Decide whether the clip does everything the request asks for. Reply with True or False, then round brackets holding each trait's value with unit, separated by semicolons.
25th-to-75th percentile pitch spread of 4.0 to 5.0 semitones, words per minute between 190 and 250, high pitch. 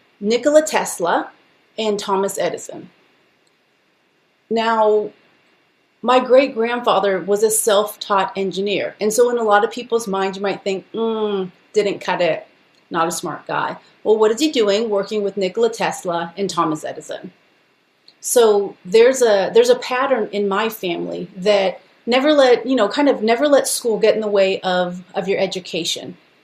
False (4.3 semitones; 160 wpm; 215 Hz)